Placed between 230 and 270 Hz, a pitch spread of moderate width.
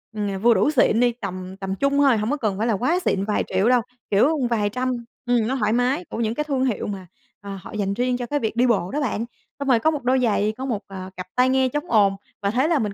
Yes: high, 235 Hz; average, 4.2 semitones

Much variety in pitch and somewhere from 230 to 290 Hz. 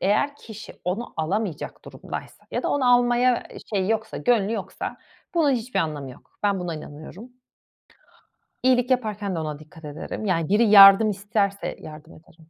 No: wide, 6.2 semitones; high, 200 Hz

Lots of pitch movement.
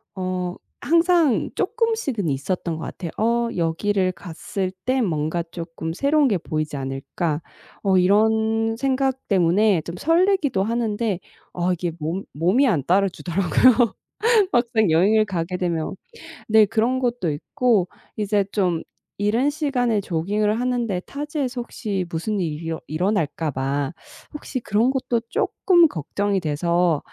Yes: wide, 6.0 semitones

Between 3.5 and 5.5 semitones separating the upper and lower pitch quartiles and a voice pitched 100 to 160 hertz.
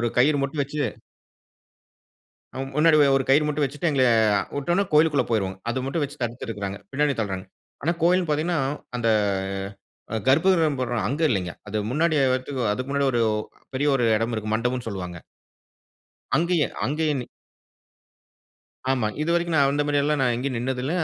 Yes: average, 4.0 semitones; low, 135 Hz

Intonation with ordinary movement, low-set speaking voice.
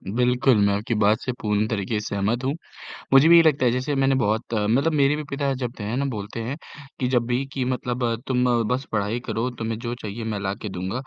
Yes: average, 3.7 semitones; low, 120 Hz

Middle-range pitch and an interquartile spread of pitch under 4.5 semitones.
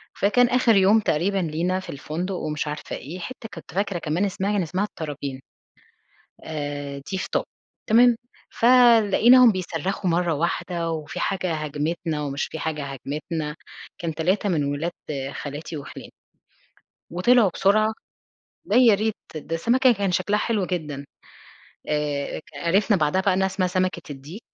No: medium, 180 Hz; average, 4.9 semitones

